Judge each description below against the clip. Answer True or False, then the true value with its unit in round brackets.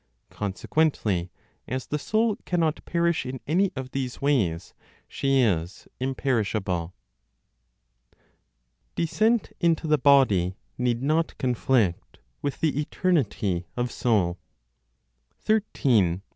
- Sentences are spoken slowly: True (105 wpm)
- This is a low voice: True (130 Hz)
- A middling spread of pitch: False (7.6 semitones)